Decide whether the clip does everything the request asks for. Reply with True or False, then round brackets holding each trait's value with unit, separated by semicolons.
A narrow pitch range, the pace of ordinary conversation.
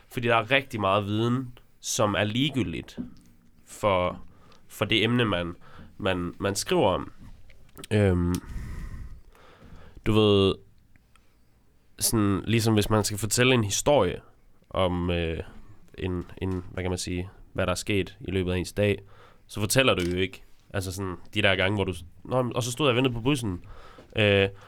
False (3.6 semitones; 165 wpm)